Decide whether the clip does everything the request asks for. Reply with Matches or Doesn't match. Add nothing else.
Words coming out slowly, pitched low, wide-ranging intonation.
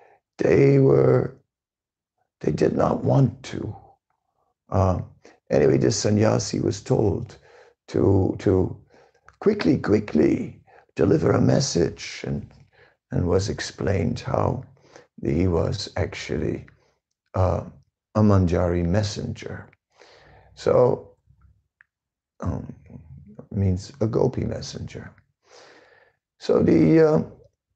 Matches